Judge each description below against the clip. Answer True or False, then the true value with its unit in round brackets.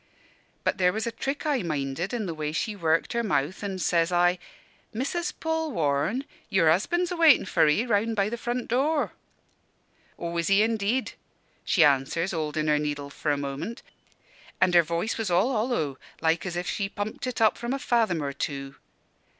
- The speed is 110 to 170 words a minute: False (185 wpm)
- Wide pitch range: True (6.7 semitones)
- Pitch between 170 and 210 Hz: True (185 Hz)